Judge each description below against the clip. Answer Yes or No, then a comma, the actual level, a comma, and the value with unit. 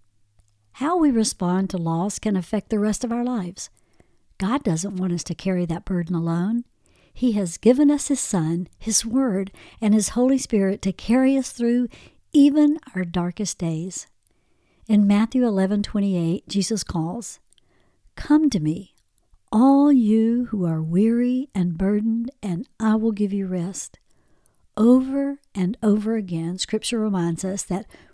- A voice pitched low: No, high, 210 Hz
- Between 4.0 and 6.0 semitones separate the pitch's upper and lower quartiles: Yes, average, 4.7 semitones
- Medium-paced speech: Yes, average, 150 wpm